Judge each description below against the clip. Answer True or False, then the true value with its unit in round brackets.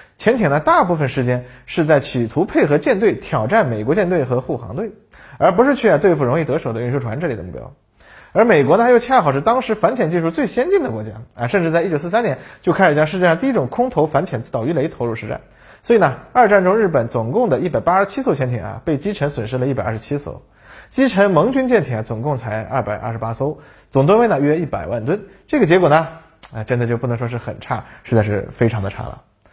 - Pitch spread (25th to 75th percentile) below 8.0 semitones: False (8.7 semitones)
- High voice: False (145 Hz)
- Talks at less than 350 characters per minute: False (360 characters per minute)